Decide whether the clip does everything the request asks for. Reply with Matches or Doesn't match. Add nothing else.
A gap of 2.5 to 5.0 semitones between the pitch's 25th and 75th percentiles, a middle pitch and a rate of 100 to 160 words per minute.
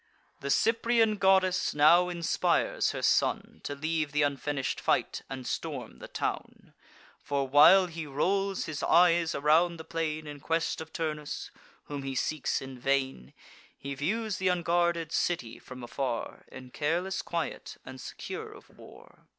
Matches